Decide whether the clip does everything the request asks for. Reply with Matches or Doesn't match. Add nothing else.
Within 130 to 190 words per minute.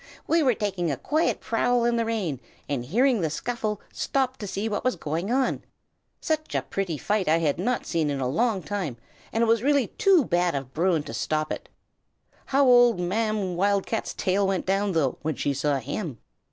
Doesn't match